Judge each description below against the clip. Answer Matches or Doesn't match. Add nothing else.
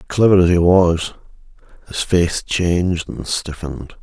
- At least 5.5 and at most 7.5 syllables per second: Doesn't match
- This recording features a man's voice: Matches